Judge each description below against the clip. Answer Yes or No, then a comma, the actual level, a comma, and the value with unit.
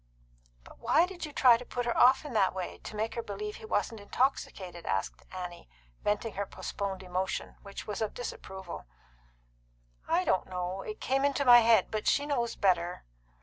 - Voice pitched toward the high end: Yes, high, 210 Hz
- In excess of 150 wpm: Yes, average, 185 wpm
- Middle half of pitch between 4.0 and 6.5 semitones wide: Yes, average, 4.6 semitones